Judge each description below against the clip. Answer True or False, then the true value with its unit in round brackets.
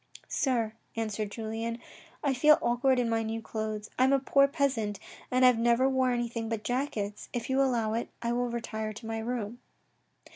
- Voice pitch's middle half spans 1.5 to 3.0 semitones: True (2.5 semitones)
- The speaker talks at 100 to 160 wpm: False (195 wpm)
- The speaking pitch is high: True (235 Hz)